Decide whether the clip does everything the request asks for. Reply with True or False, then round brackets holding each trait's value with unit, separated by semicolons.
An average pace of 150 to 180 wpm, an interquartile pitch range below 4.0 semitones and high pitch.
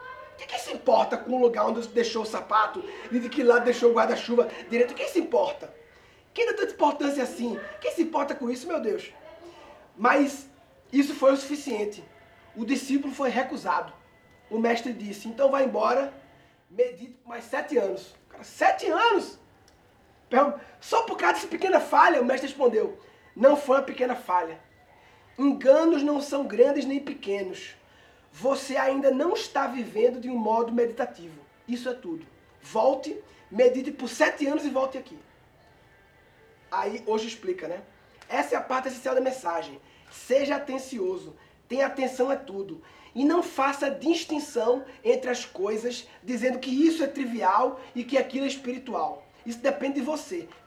True (160 wpm; 3.4 semitones; 270 Hz)